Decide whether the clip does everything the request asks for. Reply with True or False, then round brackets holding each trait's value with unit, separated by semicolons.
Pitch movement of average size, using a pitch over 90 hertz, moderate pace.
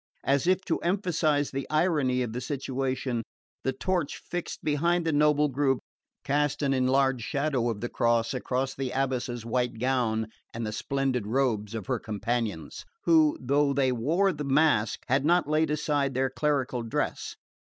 True (3.4 semitones; 135 Hz; 160 wpm)